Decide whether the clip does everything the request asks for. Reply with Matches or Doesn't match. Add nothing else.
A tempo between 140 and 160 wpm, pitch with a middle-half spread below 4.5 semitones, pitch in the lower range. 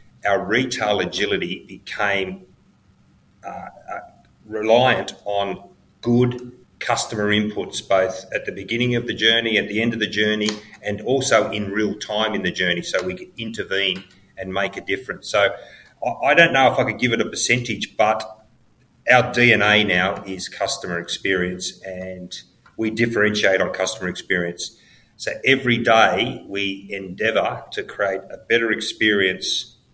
Matches